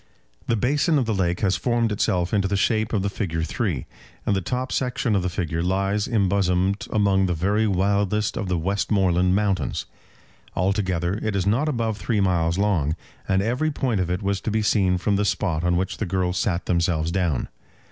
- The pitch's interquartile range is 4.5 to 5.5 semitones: No, average, 2.9 semitones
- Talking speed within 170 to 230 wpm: Yes, average, 200 wpm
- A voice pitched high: No, very low, 95 Hz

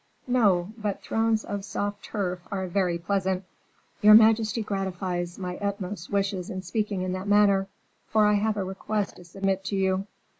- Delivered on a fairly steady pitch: Yes, narrow, 1.9 semitones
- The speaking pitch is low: No, high, 195 Hz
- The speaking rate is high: No, average, 165 wpm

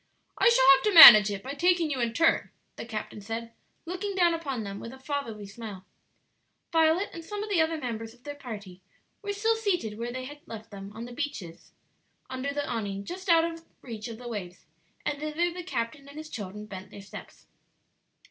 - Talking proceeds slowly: No, fast, 205 wpm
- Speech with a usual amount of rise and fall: No, wide, 7.2 semitones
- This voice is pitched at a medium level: No, very high, 260 Hz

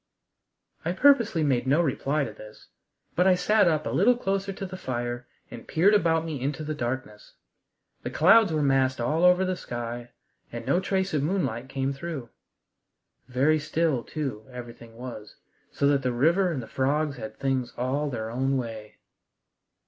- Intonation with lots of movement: Yes, wide, 5.7 semitones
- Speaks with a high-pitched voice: No, medium, 140 Hz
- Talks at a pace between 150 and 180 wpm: Yes, average, 170 wpm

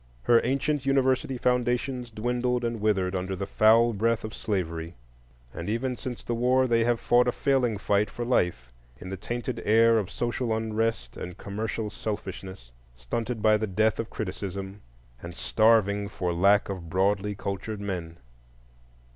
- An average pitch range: Yes, average, 3.7 semitones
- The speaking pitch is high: No, low, 110 Hz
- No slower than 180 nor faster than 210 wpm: No, average, 155 wpm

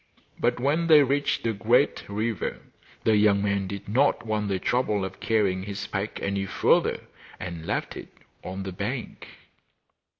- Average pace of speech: Yes, average, 160 wpm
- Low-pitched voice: Yes, low, 105 Hz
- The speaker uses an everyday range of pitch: Yes, average, 3.4 semitones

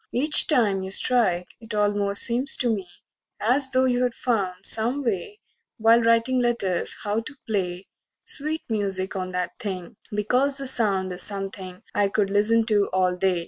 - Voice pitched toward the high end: Yes, high, 210 Hz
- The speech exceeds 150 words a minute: Yes, average, 170 wpm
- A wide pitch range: No, average, 4.3 semitones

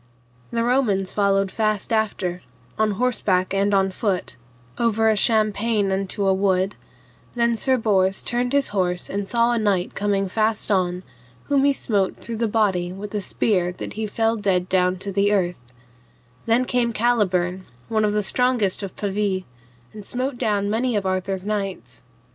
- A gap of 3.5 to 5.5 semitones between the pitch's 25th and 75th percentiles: No, average, 3.0 semitones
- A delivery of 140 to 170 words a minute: Yes, average, 165 wpm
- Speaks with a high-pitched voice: Yes, high, 205 Hz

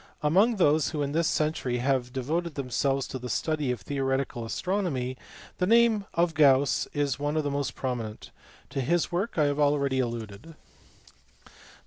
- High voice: No, medium, 145 Hz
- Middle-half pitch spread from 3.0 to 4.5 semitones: Yes, average, 3.8 semitones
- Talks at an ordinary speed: Yes, average, 165 wpm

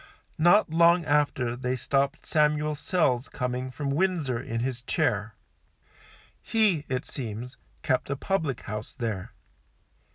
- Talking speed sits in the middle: No, slow, 125 wpm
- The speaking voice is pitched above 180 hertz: No, low, 135 Hz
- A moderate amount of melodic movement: Yes, average, 4.2 semitones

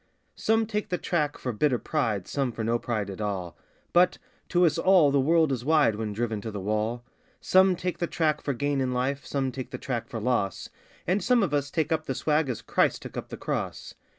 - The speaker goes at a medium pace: No, fast, 230 wpm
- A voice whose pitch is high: No, medium, 140 Hz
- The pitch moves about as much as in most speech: No, wide, 5.7 semitones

